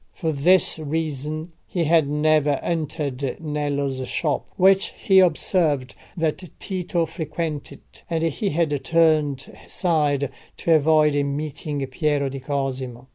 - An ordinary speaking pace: No, slow, 120 wpm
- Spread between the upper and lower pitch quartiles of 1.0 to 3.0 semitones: Yes, average, 2.7 semitones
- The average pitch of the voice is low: No, medium, 150 Hz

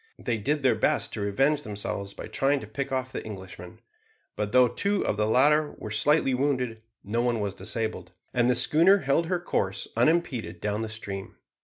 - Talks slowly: No, average, 190 wpm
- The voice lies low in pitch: Yes, low, 120 Hz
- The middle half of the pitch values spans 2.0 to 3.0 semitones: No, average, 5.0 semitones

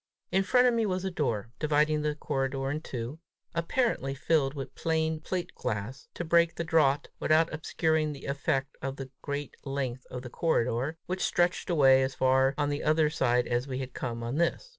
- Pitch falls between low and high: Yes, medium, 145 Hz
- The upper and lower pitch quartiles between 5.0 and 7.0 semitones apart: No, average, 3.5 semitones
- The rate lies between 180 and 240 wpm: Yes, average, 195 wpm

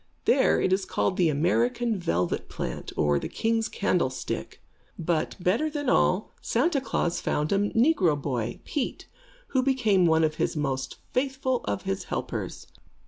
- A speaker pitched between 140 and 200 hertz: Yes, medium, 185 Hz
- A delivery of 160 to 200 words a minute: No, average, 150 wpm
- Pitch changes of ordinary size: No, wide, 8.5 semitones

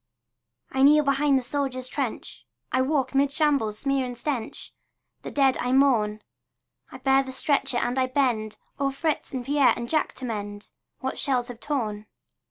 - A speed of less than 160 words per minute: No, average, 175 wpm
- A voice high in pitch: Yes, very high, 265 Hz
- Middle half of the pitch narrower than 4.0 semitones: Yes, narrow, 2.5 semitones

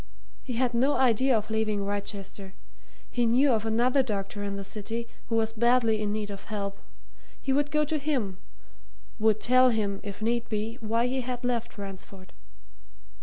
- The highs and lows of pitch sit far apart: No, average, 3.4 semitones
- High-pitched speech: Yes, high, 225 Hz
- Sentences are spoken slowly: No, average, 170 wpm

